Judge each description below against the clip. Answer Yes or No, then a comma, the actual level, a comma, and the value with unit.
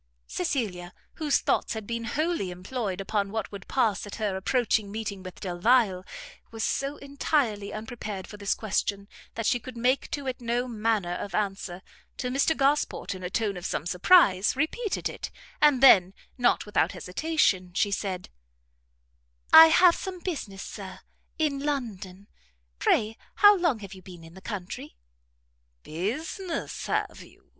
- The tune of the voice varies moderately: No, wide, 6.1 semitones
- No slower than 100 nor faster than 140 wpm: No, average, 155 wpm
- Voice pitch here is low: No, high, 215 Hz